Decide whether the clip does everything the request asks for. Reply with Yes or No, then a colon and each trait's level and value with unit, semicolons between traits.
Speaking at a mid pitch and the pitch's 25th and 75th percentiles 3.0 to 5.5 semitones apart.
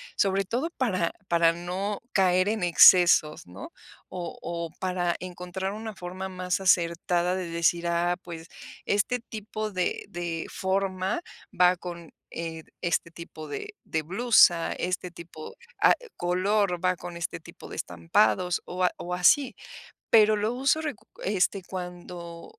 No: medium, 180 Hz; narrow, 2.4 semitones